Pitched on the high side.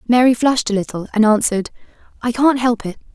Yes: high, 230 Hz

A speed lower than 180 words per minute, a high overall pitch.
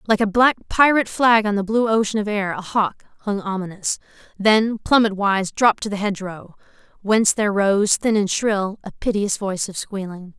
No: average, 190 wpm; high, 205 Hz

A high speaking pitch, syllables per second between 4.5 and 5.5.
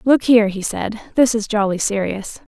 Yes: high, 215 Hz; 5.1 syllables/s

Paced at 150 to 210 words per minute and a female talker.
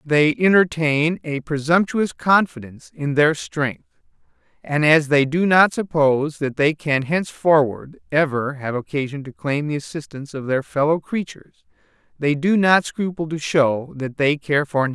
No: average, 170 wpm; male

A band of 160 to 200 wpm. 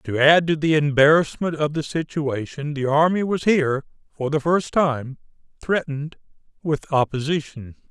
No: average, 145 wpm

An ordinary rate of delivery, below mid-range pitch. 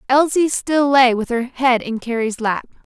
No: average, 185 wpm; very high, 250 Hz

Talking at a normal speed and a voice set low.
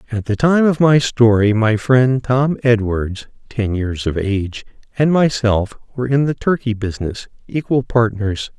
Yes: average, 160 wpm; low, 120 Hz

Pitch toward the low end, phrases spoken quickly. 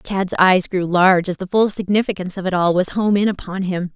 No: high, 190 Hz; fast, 245 wpm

